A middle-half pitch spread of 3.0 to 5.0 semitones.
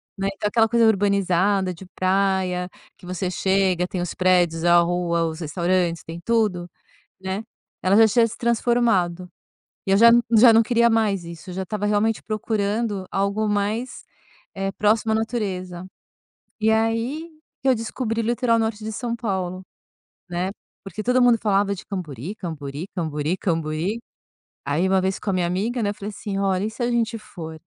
Yes: average, 3.7 semitones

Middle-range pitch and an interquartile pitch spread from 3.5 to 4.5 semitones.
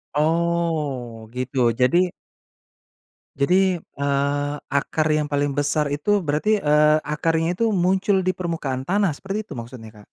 Yes: medium, 150 Hz; average, 3.8 semitones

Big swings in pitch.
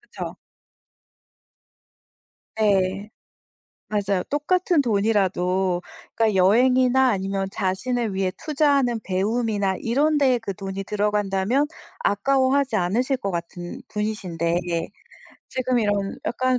No: average, 4.9 semitones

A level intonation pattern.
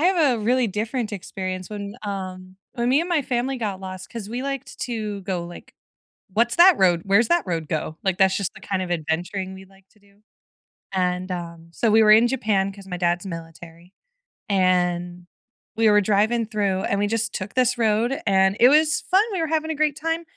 No: average, 4.4 semitones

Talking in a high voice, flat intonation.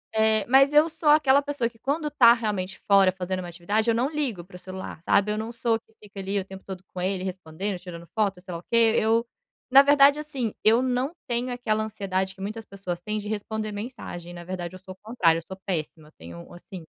No: high, 210 Hz; average, 4.4 semitones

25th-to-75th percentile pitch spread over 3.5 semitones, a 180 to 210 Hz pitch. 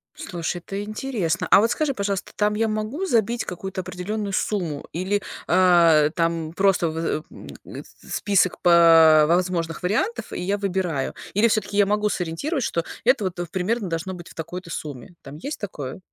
Yes: average, 3.9 semitones; medium, 185 Hz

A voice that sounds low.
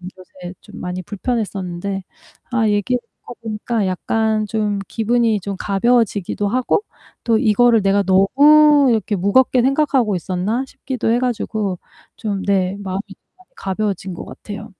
No: high, 210 Hz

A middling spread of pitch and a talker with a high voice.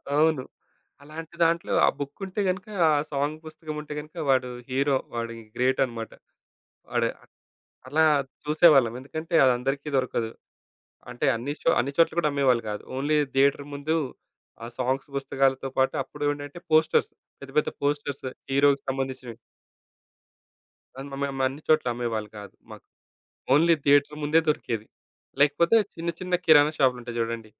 No: average, 3.0 semitones; medium, 140 Hz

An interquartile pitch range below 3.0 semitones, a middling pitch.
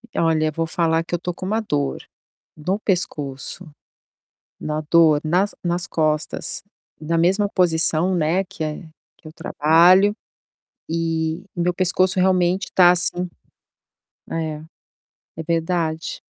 Yes: narrow, 2.4 semitones; medium, 170 Hz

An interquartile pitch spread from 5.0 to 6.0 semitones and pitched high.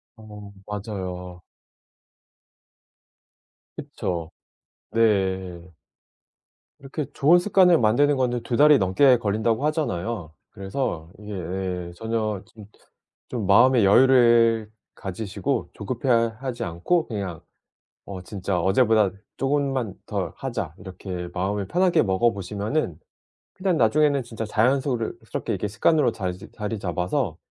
No: average, 5.3 semitones; low, 110 Hz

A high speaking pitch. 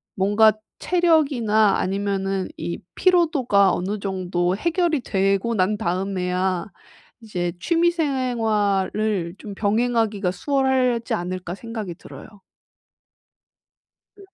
Yes: high, 210 Hz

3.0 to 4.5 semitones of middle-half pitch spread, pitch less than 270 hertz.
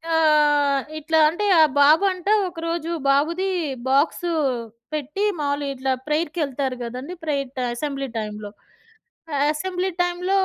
No: average, 3.5 semitones; very high, 300 Hz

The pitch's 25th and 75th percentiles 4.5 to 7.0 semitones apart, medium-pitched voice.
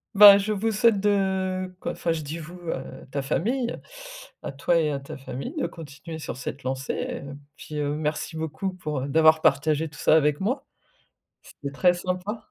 Yes: average, 4.8 semitones; medium, 160 Hz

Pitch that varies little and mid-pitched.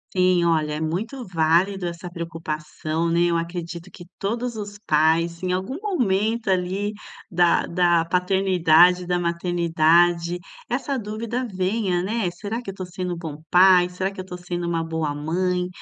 Yes: narrow, 2.3 semitones; medium, 180 Hz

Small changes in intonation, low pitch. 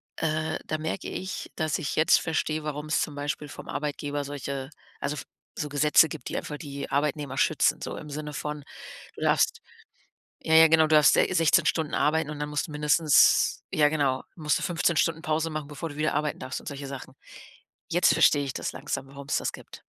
No: narrow, 1.6 semitones; medium, 150 Hz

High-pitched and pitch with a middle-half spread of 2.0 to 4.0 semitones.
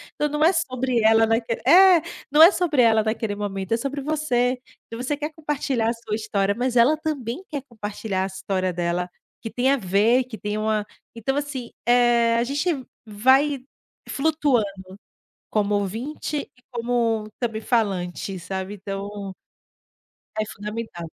No: high, 230 Hz; average, 4.8 semitones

